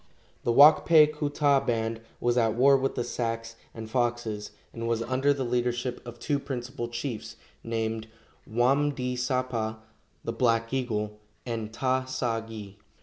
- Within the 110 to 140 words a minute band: No, average, 155 wpm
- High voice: No, low, 120 Hz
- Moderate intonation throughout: No, narrow, 2.3 semitones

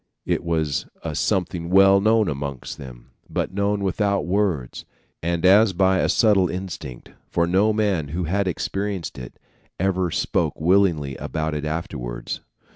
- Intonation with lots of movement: No, average, 4.2 semitones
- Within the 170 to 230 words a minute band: No, average, 145 wpm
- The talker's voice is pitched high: No, very low, 90 Hz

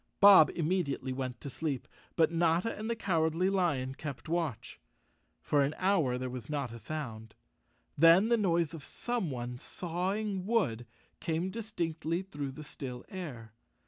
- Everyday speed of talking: Yes, average, 150 wpm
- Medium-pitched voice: Yes, medium, 160 Hz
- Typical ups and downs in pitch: No, wide, 5.9 semitones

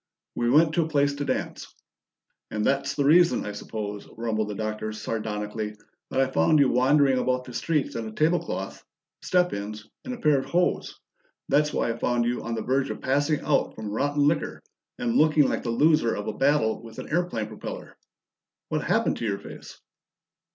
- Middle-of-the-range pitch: No, low, 130 Hz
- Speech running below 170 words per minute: No, average, 195 wpm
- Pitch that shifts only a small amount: No, wide, 5.5 semitones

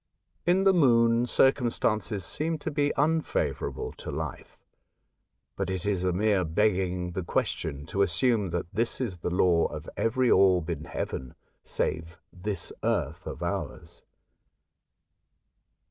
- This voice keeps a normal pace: No, slow, 130 wpm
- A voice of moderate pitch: No, very low, 95 Hz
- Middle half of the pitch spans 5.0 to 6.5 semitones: Yes, wide, 5.4 semitones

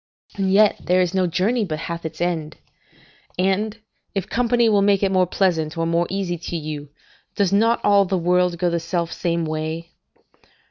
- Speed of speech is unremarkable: Yes, average, 185 wpm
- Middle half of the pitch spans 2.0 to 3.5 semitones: Yes, average, 2.9 semitones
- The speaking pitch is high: No, medium, 180 Hz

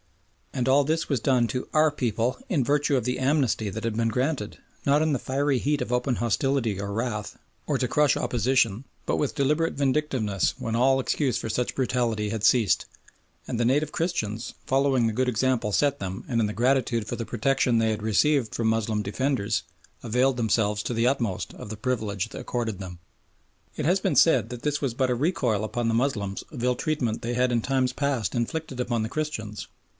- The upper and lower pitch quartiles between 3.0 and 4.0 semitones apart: Yes, average, 3.7 semitones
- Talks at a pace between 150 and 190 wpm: No, average, 200 wpm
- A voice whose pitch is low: Yes, low, 125 Hz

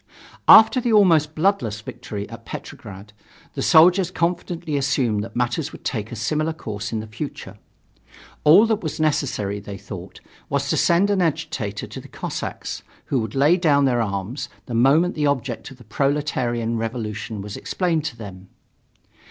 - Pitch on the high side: No, low, 135 Hz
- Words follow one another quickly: No, average, 165 wpm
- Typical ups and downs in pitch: No, wide, 6.7 semitones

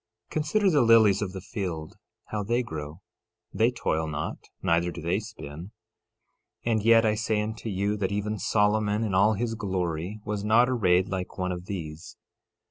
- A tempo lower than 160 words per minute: No, average, 175 wpm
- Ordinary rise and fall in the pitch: Yes, average, 3.6 semitones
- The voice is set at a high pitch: No, low, 105 Hz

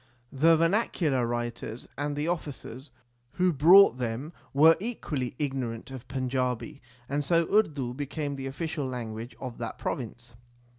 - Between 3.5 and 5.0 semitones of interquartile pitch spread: Yes, average, 4.1 semitones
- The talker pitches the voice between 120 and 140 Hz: Yes, low, 135 Hz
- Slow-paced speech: No, average, 145 wpm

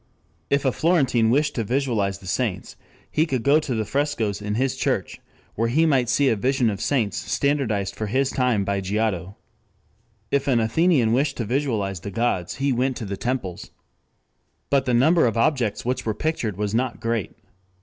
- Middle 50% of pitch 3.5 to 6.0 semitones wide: Yes, average, 4.7 semitones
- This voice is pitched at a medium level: No, low, 120 Hz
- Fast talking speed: No, average, 185 wpm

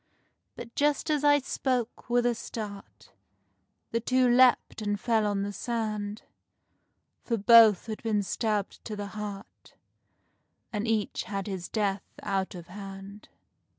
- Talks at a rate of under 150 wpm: Yes, average, 140 wpm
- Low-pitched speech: No, high, 215 Hz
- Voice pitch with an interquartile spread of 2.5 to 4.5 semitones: Yes, average, 2.8 semitones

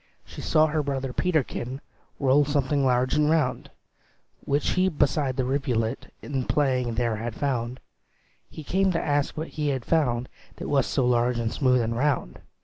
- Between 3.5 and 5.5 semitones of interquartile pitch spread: No, average, 3.1 semitones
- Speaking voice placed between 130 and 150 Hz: Yes, low, 135 Hz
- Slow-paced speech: No, average, 170 wpm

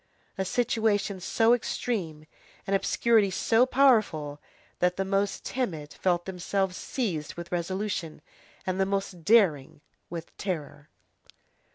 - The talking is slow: Yes, slow, 120 wpm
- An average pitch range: Yes, average, 4.0 semitones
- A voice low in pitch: No, high, 190 Hz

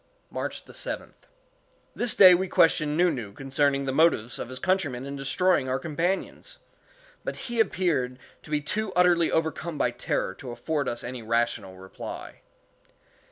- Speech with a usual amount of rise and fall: No, wide, 5.7 semitones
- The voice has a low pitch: No, medium, 150 Hz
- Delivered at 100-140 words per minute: No, average, 155 wpm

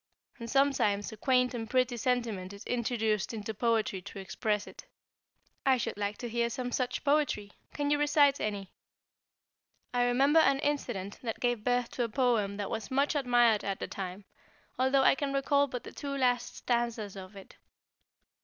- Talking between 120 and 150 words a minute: No, average, 175 wpm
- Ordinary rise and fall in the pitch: Yes, average, 4.1 semitones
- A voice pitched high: Yes, high, 240 Hz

